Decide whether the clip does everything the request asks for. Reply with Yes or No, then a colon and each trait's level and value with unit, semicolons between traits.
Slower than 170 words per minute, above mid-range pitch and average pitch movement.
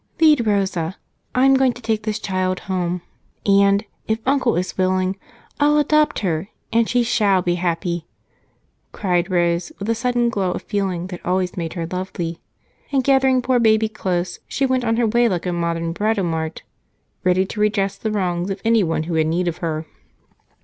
No: average, 175 wpm; high, 195 Hz; average, 4.6 semitones